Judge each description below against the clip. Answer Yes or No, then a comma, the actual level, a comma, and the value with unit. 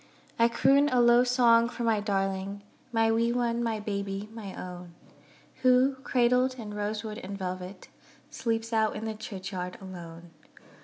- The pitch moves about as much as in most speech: Yes, average, 3.4 semitones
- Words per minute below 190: Yes, average, 150 wpm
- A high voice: Yes, high, 220 Hz